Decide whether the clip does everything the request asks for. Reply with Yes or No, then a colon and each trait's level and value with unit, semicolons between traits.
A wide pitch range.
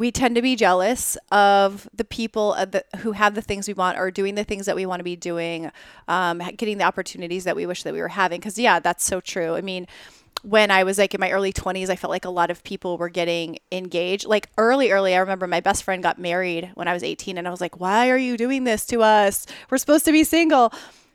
No: average, 3.4 semitones